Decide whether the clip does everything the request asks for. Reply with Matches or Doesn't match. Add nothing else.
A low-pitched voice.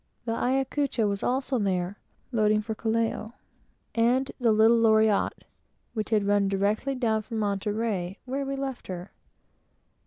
Doesn't match